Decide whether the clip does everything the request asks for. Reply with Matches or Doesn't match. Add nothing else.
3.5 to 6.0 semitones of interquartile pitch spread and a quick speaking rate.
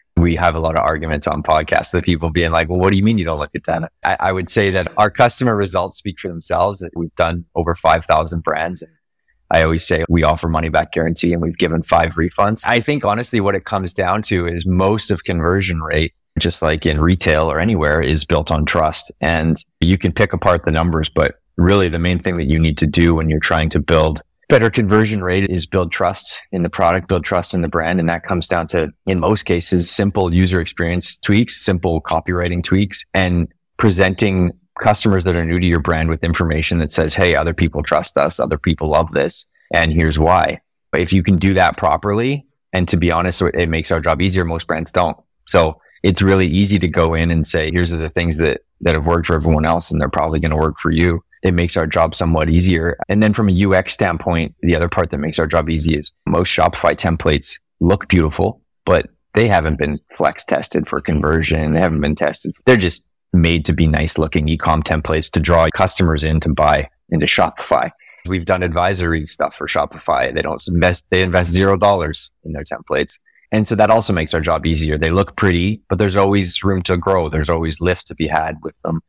Doesn't match